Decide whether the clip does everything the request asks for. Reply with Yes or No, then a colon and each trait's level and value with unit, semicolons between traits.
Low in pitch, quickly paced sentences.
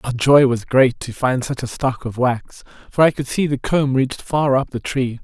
Yes: low, 130 Hz; fast, 250 wpm